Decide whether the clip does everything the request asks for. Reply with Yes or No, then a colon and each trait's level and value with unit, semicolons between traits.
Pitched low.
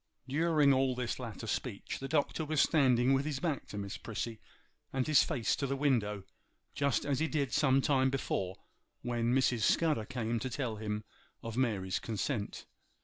Yes: low, 130 Hz